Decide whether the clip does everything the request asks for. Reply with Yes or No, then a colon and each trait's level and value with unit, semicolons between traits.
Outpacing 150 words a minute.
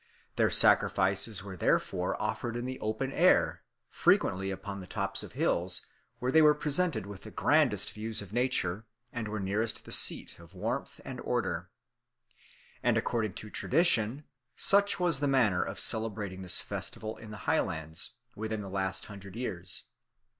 Yes: average, 160 wpm